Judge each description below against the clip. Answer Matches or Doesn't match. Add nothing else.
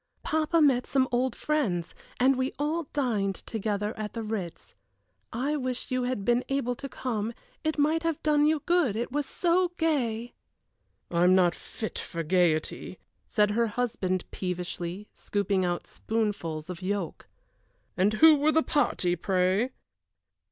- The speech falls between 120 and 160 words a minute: Matches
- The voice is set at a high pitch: Matches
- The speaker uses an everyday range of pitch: Doesn't match